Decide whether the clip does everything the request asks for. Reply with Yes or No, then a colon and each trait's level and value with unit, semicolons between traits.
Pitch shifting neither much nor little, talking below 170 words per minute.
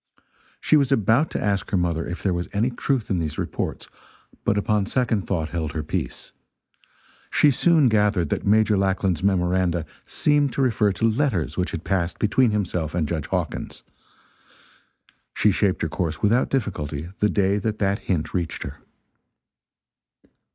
Yes: average, 4.2 semitones; average, 160 wpm